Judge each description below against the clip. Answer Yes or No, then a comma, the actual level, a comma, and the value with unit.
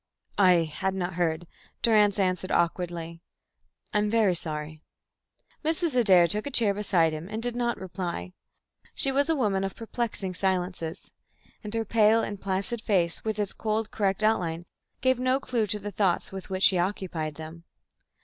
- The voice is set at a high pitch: Yes, high, 195 Hz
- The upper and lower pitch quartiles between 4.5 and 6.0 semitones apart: No, average, 4.1 semitones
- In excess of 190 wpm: No, average, 170 wpm